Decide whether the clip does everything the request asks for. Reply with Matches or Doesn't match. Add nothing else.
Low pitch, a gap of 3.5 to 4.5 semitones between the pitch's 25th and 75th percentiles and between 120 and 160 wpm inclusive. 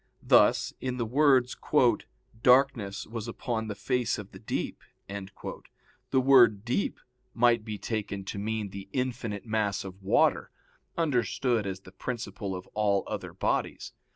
Matches